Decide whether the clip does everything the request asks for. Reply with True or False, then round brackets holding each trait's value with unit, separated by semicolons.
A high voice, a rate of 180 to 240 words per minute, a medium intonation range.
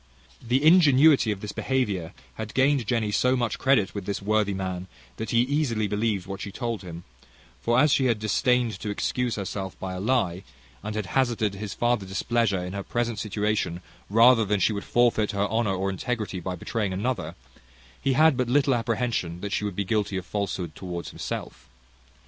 False (110 Hz; 190 wpm; 3.9 semitones)